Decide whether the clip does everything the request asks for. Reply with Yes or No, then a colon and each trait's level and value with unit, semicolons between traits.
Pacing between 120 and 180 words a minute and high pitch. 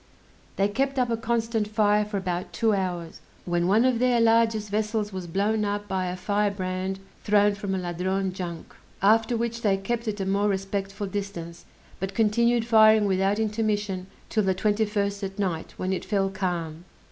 Yes: average, 175 wpm; high, 205 Hz